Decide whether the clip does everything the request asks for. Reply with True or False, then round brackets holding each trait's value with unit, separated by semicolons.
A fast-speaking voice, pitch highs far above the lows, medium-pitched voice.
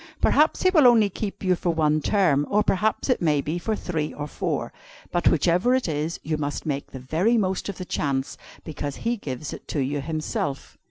True (210 wpm; 5.7 semitones; 165 Hz)